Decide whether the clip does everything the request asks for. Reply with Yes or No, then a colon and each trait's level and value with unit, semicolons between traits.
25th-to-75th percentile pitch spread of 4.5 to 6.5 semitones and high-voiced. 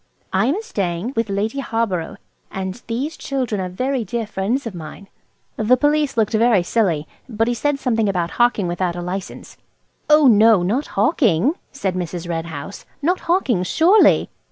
Yes: wide, 5.6 semitones; high, 220 Hz